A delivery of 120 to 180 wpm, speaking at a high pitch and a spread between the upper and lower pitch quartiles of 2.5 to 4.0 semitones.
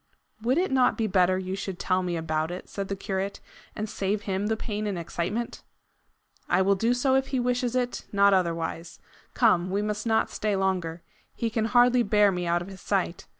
No: fast, 205 wpm; high, 200 Hz; average, 3.6 semitones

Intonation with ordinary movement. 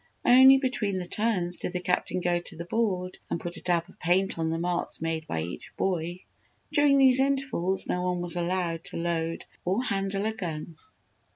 Yes: average, 3.5 semitones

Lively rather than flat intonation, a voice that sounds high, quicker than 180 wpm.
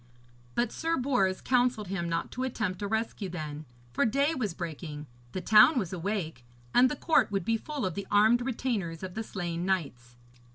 Yes: wide, 6.2 semitones; high, 200 Hz; average, 190 wpm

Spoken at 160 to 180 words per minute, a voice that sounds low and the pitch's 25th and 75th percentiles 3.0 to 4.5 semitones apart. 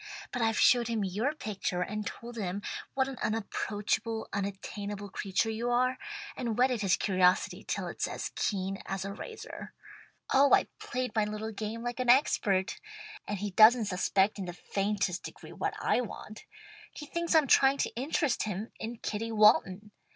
No: average, 170 wpm; high, 215 Hz; average, 3.4 semitones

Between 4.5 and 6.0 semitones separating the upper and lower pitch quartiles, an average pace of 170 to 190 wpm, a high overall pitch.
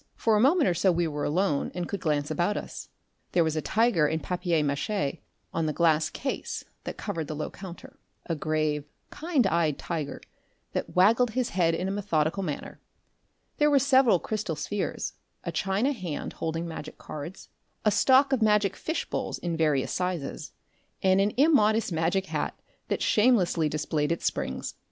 No: average, 5.2 semitones; average, 175 wpm; medium, 175 Hz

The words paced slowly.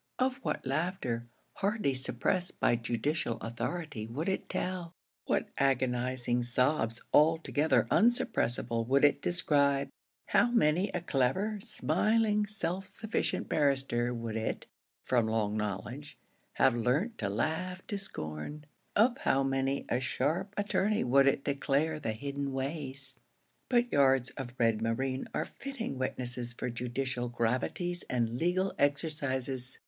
Yes: slow, 130 wpm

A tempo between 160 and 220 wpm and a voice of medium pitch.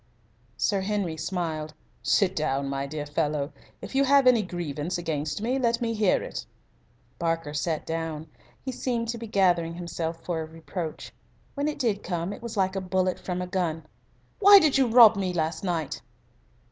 Yes: average, 180 wpm; medium, 180 Hz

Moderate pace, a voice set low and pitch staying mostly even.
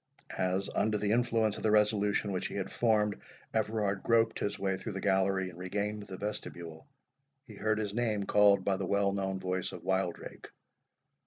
Yes: average, 180 wpm; low, 100 Hz; narrow, 1.9 semitones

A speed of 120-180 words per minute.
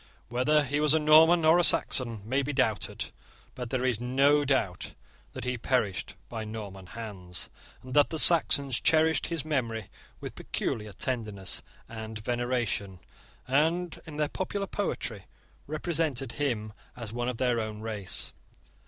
Yes: average, 150 wpm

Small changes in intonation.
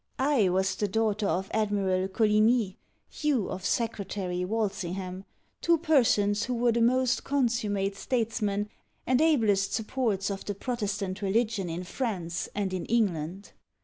No: average, 3.4 semitones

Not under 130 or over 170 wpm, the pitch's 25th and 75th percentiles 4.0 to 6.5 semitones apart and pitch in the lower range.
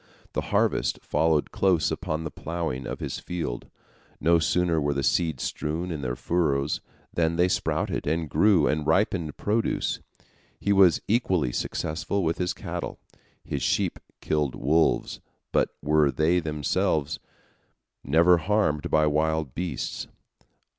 No: slow, 135 wpm; average, 2.8 semitones; very low, 80 Hz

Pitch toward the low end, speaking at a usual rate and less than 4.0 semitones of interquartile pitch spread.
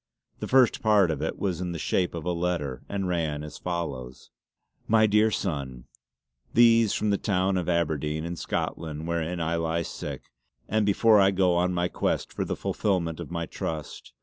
Yes: very low, 85 Hz; average, 185 wpm; average, 3.6 semitones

